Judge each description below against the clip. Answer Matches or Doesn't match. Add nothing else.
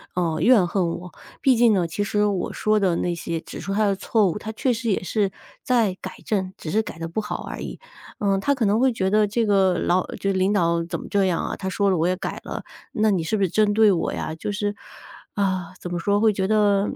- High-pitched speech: Matches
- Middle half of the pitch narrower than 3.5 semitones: Matches